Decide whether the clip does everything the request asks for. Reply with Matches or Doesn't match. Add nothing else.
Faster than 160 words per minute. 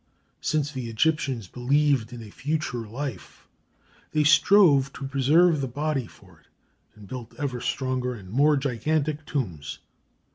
Doesn't match